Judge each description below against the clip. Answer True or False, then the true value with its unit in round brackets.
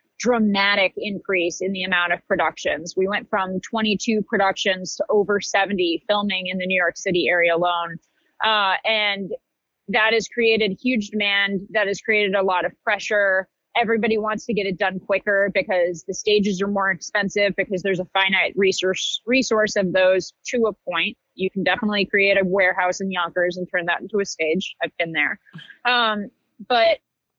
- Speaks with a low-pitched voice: False (195 Hz)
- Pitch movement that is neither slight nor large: False (2.3 semitones)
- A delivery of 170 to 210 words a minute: True (175 wpm)